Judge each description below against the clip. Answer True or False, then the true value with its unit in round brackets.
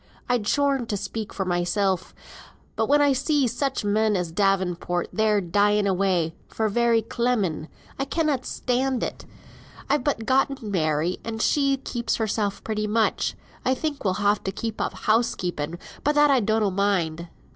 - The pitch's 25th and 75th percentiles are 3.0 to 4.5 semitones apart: False (4.9 semitones)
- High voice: True (215 Hz)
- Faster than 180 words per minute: False (165 wpm)